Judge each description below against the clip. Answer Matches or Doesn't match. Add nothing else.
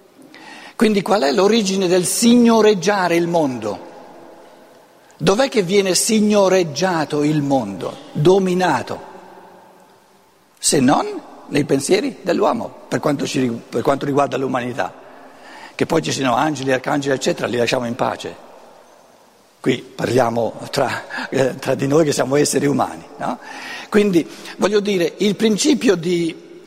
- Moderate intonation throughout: Doesn't match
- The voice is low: Doesn't match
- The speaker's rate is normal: Matches